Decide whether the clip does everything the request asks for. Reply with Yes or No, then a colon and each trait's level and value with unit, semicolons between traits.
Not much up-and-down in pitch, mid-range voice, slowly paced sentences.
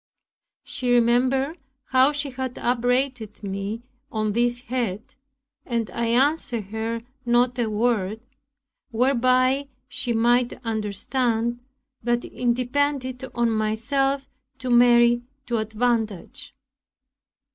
No: narrow, 2.2 semitones; high, 240 Hz; slow, 105 wpm